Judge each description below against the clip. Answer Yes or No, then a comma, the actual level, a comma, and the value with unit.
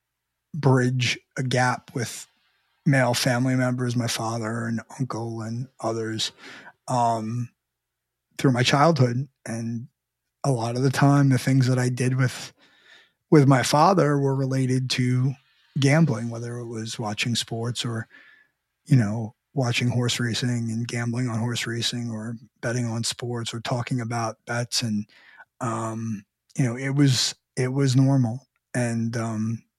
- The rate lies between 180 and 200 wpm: No, average, 145 wpm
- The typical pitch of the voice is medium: No, low, 120 Hz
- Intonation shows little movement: Yes, narrow, 2.3 semitones